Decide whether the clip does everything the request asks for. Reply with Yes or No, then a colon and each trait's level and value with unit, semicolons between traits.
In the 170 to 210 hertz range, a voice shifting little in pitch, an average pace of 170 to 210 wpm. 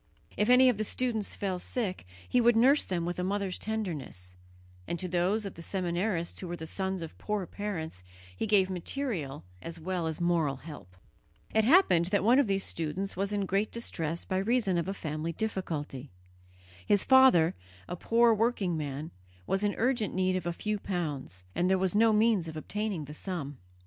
No: medium, 185 Hz; average, 4.3 semitones; average, 190 wpm